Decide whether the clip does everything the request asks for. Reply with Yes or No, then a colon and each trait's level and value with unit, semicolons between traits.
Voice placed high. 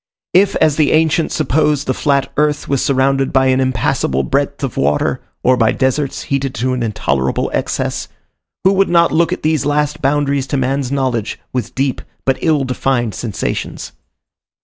No: low, 135 Hz